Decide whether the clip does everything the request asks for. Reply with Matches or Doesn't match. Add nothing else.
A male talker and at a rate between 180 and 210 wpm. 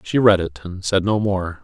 Doesn't match